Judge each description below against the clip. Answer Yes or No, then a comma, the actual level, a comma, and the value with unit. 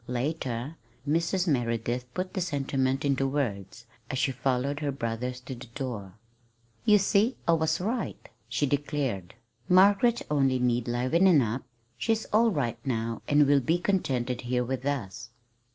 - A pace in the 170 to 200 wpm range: No, average, 150 wpm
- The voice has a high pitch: No, low, 135 Hz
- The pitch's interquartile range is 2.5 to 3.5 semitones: No, average, 5.0 semitones